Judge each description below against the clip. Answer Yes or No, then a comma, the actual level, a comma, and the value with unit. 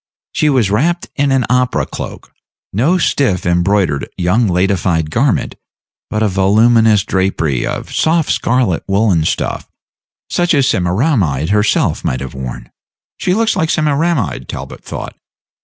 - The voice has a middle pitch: No, low, 105 Hz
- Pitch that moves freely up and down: Yes, wide, 7.5 semitones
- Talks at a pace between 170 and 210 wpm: No, slow, 135 wpm